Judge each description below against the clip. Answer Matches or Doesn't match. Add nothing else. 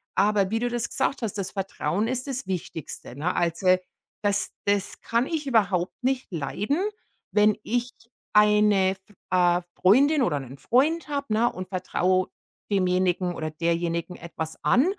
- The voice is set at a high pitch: Matches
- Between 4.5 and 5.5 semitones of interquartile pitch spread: Matches